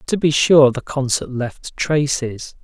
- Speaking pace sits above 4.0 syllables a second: No, 3.7 syllables/s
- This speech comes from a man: Yes, male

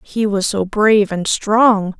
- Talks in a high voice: Yes, high, 205 Hz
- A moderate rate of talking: Yes, average, 180 wpm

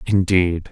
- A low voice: Yes, very low, 90 Hz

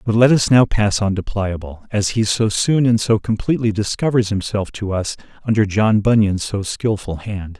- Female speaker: No, male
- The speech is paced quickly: No, average, 195 wpm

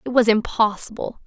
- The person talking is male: No, female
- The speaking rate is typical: Yes, average, 145 wpm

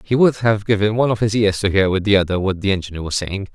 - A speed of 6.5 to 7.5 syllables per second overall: Yes, 6.7 syllables/s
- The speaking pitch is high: No, low, 100 Hz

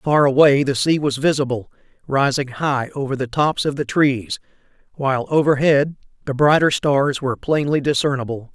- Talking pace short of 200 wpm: Yes, average, 155 wpm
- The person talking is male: Yes, male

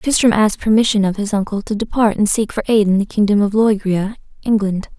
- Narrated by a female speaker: Yes, female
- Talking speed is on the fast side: Yes, fast, 215 wpm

